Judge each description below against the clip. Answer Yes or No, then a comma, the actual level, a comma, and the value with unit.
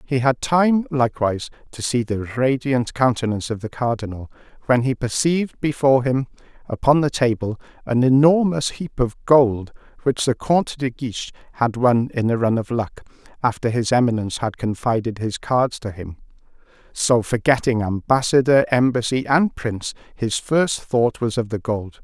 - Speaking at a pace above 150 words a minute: Yes, average, 160 wpm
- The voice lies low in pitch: Yes, low, 125 Hz